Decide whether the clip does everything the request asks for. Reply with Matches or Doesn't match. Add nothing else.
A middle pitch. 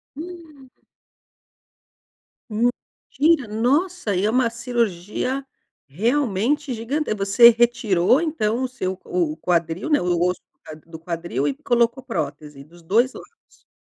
Doesn't match